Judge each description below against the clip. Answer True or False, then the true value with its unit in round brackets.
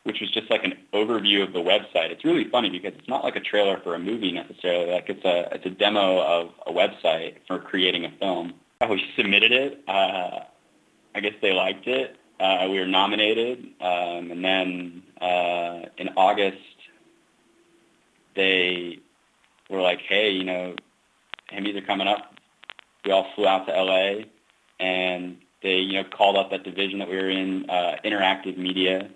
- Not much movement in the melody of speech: True (1.3 semitones)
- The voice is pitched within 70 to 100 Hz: True (95 Hz)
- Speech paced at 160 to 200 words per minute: True (175 wpm)